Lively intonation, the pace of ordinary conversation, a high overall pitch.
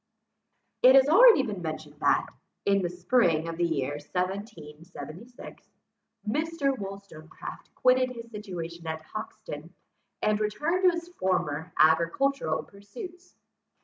No: wide, 7.8 semitones; slow, 115 wpm; high, 200 Hz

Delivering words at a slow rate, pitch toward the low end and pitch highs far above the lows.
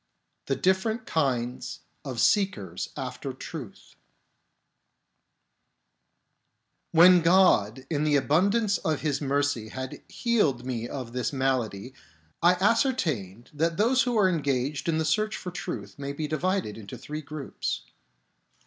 No: slow, 125 wpm; medium, 145 Hz; wide, 6.3 semitones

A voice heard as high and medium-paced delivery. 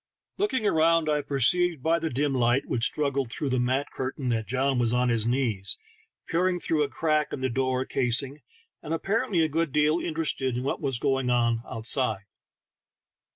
No: low, 135 Hz; average, 185 wpm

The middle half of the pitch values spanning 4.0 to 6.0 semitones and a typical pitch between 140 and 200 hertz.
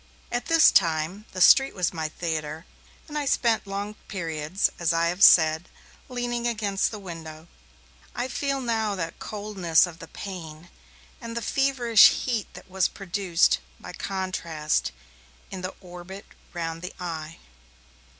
Yes: average, 4.9 semitones; medium, 185 Hz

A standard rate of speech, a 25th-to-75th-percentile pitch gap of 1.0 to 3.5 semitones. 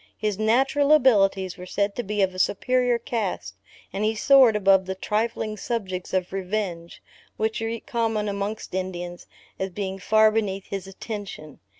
Yes: average, 160 wpm; average, 2.8 semitones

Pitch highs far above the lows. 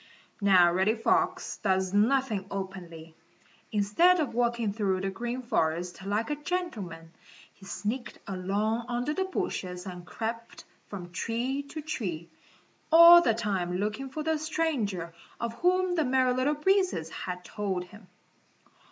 Yes: wide, 7.0 semitones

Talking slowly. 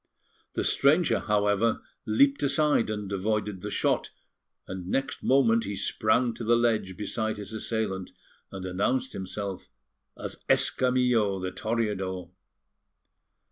Yes: slow, 120 wpm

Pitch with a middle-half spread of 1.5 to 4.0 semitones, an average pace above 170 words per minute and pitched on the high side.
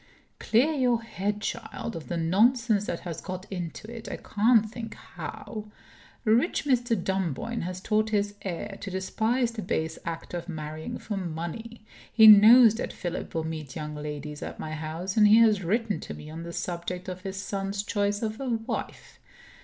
No: average, 4.8 semitones; average, 180 wpm; high, 200 Hz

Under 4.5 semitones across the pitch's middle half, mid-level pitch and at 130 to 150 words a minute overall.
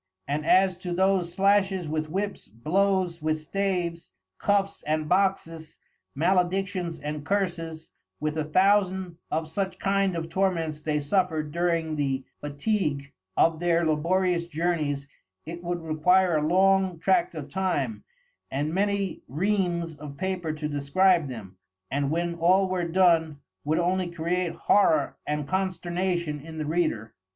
Yes: average, 3.5 semitones; medium, 170 Hz; average, 140 wpm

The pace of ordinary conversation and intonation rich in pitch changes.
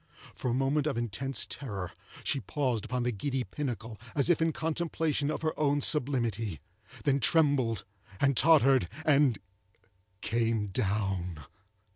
No: slow, 130 wpm; wide, 5.7 semitones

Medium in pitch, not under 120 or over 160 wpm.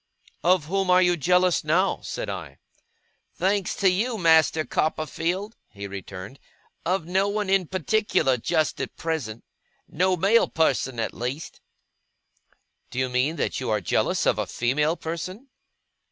Yes: medium, 165 Hz; average, 145 wpm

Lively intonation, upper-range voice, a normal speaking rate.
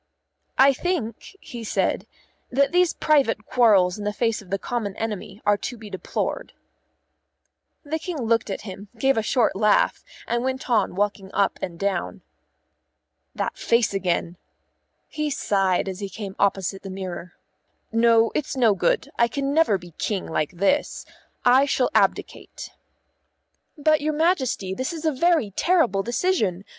Yes: wide, 5.8 semitones; high, 225 Hz; average, 155 wpm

